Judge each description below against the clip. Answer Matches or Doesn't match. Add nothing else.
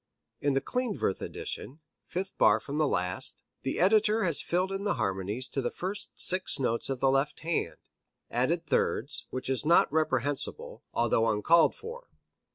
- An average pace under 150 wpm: Doesn't match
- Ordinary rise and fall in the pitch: Doesn't match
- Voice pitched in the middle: Matches